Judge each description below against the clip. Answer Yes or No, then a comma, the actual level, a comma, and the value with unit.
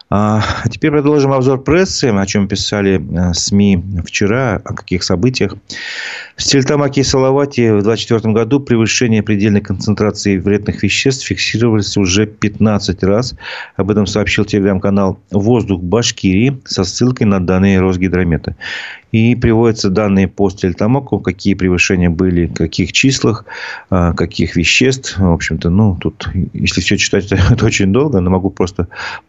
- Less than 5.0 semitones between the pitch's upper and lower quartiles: Yes, average, 3.3 semitones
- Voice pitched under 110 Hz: Yes, low, 100 Hz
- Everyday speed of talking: Yes, average, 135 wpm